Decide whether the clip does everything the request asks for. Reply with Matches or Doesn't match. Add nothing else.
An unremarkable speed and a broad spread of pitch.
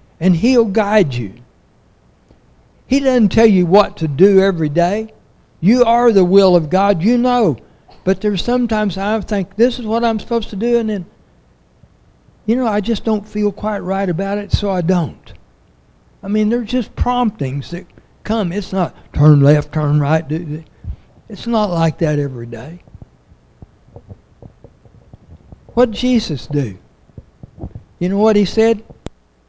Matches